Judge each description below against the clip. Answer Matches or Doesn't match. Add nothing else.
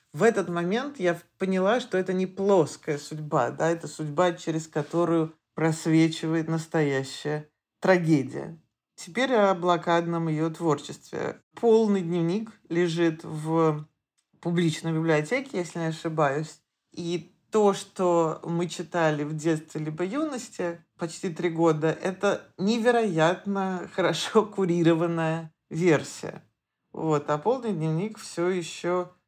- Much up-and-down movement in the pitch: Doesn't match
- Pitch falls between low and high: Matches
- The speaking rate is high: Doesn't match